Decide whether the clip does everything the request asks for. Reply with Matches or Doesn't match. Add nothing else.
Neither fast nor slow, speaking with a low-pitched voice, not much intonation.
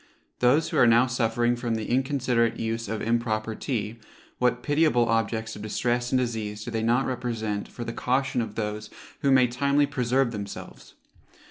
Matches